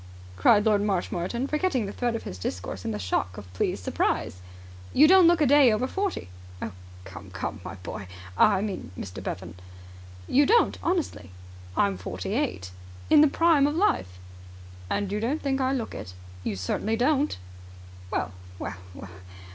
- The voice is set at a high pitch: Yes, high, 210 Hz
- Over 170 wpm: No, average, 165 wpm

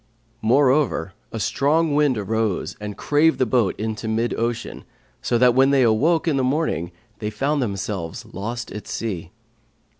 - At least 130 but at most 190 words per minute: Yes, average, 155 wpm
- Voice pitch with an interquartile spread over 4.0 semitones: Yes, average, 4.6 semitones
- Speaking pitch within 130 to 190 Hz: No, low, 120 Hz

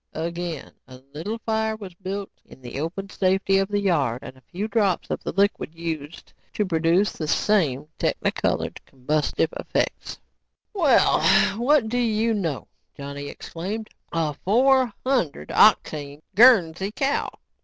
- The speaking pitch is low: No, medium, 185 Hz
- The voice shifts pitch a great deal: Yes, wide, 5.9 semitones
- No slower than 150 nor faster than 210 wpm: No, average, 140 wpm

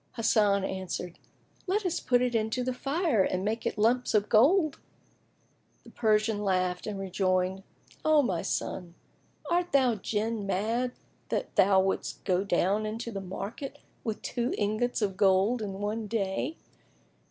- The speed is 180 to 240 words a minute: No, average, 155 wpm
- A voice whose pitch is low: No, high, 215 Hz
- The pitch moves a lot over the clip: No, average, 4.2 semitones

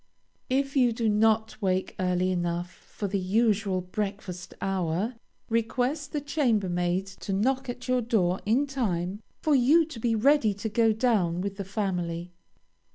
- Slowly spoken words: No, average, 155 wpm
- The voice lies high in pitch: Yes, high, 210 Hz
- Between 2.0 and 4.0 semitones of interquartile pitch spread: No, average, 4.8 semitones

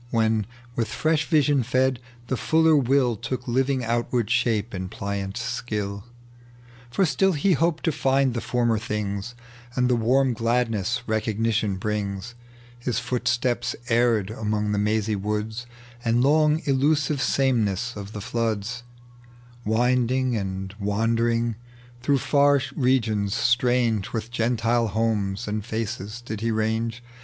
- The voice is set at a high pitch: No, low, 115 Hz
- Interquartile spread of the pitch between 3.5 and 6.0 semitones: No, average, 3.0 semitones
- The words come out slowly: Yes, slow, 130 wpm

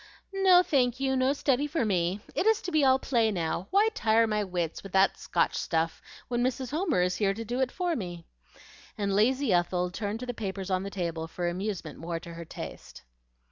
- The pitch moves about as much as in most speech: No, wide, 6.7 semitones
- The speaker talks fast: Yes, fast, 215 wpm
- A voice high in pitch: Yes, high, 210 Hz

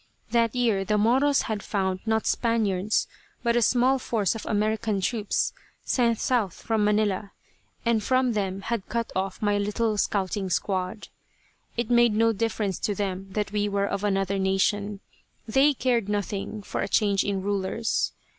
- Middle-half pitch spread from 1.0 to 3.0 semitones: Yes, average, 2.7 semitones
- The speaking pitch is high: Yes, high, 210 Hz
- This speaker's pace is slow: No, average, 160 wpm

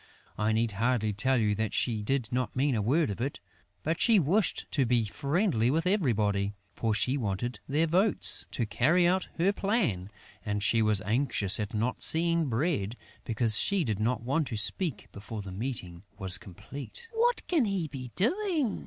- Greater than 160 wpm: Yes, average, 180 wpm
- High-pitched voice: No, low, 125 Hz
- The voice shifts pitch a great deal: Yes, wide, 7.6 semitones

